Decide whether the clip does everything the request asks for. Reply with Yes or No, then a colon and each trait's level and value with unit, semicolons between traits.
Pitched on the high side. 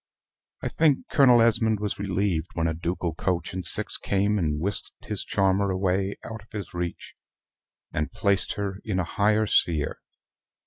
No: very low, 95 Hz